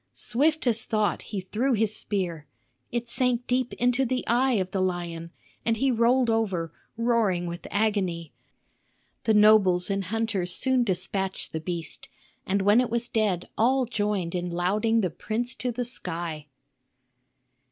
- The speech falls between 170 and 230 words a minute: No, average, 150 wpm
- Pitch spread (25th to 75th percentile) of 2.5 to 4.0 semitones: No, average, 4.8 semitones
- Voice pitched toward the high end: Yes, high, 210 Hz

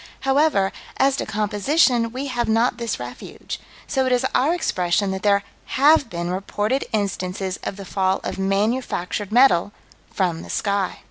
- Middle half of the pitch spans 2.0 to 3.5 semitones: No, average, 5.2 semitones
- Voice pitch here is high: Yes, high, 205 Hz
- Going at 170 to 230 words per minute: No, average, 155 wpm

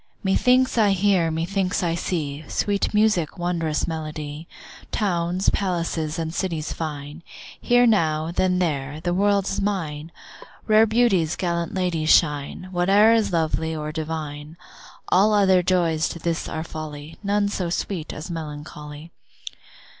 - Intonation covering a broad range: No, average, 3.7 semitones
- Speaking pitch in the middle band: Yes, medium, 170 Hz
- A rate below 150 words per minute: Yes, slow, 135 wpm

